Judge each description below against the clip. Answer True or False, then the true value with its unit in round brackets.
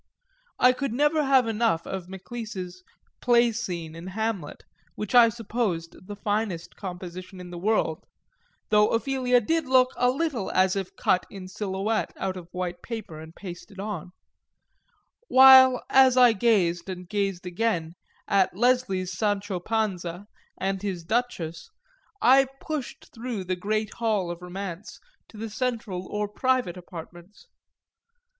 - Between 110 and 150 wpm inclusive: True (140 wpm)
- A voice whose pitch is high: True (205 Hz)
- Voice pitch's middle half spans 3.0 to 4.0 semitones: False (4.7 semitones)